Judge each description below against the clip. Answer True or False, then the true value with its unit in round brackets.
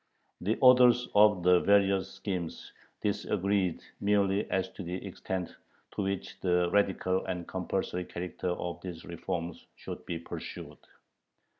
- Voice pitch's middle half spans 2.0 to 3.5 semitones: True (2.4 semitones)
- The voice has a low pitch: True (95 Hz)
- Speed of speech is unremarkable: False (130 wpm)